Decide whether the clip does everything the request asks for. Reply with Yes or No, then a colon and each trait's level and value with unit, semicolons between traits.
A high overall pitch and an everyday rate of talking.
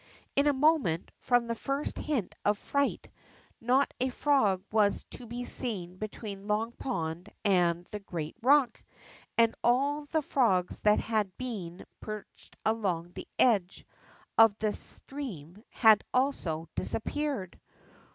No: high, 220 Hz; slow, 130 wpm